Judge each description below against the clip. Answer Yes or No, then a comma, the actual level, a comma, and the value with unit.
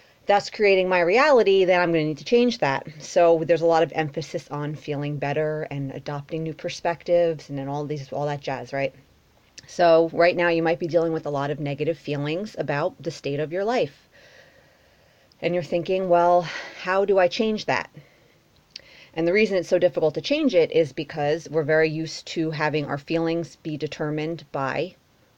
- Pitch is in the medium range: Yes, medium, 165 Hz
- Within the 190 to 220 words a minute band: Yes, average, 195 wpm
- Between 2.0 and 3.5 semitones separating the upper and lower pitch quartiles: Yes, average, 2.8 semitones